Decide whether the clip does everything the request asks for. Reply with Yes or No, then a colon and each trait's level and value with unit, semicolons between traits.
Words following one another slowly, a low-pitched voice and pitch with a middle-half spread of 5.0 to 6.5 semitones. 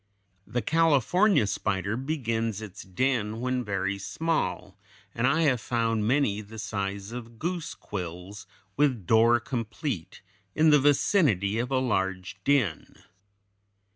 Yes: slow, 125 wpm; low, 115 Hz; average, 5.3 semitones